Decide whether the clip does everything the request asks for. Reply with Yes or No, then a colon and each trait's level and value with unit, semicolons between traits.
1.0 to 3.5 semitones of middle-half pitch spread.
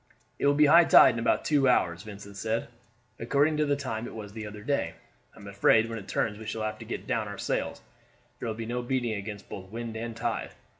Yes: average, 3.0 semitones